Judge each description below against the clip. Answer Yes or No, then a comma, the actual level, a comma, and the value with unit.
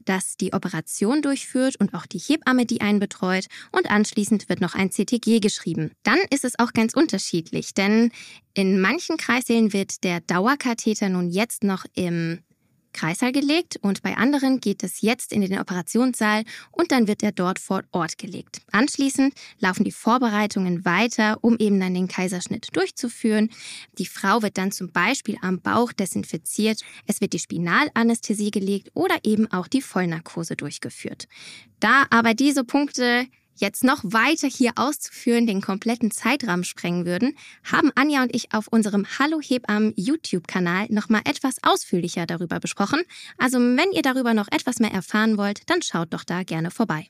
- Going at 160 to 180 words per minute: Yes, average, 165 wpm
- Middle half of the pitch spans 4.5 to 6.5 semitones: Yes, average, 4.8 semitones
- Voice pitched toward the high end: Yes, high, 215 Hz